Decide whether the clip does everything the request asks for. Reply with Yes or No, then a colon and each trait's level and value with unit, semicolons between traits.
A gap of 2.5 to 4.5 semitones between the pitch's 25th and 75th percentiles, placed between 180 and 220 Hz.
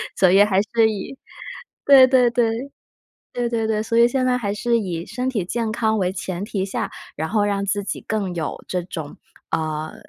Yes: average, 3.9 semitones; high, 210 Hz